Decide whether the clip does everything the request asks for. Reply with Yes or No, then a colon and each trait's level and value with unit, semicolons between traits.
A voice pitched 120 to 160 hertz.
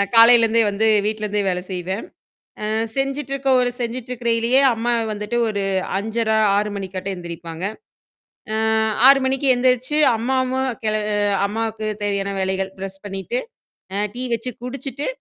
No: high, 225 Hz